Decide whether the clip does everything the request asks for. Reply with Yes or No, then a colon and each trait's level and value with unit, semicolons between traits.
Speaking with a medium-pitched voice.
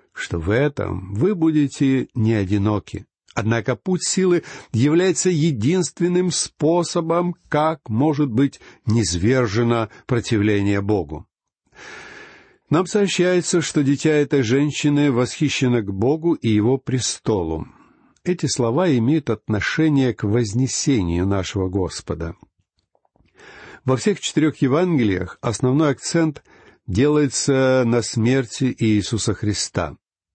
No: low, 130 Hz